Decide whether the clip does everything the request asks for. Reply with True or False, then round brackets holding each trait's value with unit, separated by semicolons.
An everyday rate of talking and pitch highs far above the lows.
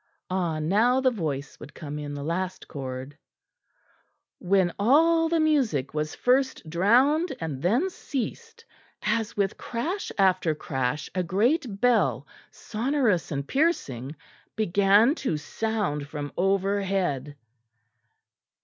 False (115 wpm; 8.5 semitones)